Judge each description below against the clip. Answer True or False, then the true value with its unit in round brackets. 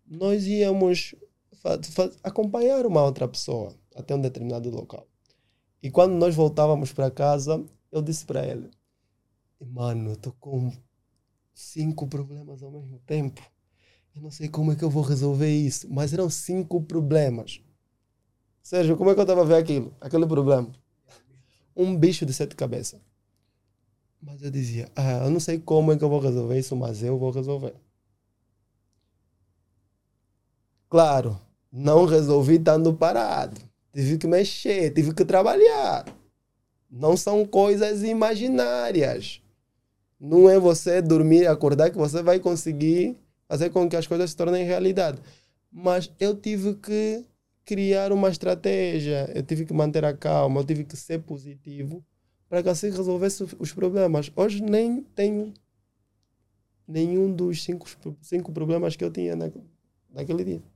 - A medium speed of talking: True (145 wpm)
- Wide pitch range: True (6.5 semitones)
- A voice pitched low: False (150 Hz)